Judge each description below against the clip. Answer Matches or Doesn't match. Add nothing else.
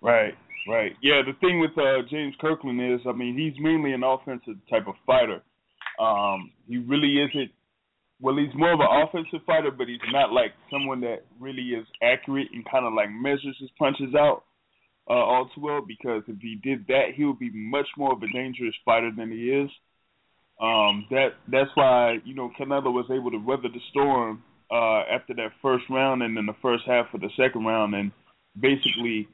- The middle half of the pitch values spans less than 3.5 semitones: Matches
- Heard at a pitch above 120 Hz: Matches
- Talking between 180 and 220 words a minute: Matches